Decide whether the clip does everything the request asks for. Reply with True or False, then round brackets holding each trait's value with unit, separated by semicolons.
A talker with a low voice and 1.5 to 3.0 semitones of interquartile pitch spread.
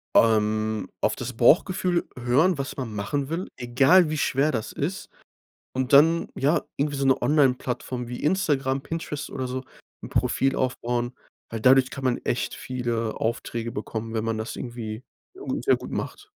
False (130 Hz; 3.7 semitones)